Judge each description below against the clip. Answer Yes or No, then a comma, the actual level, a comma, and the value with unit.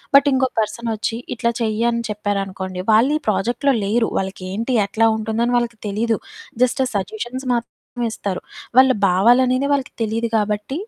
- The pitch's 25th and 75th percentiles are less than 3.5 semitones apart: Yes, average, 2.8 semitones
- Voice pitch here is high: Yes, high, 230 Hz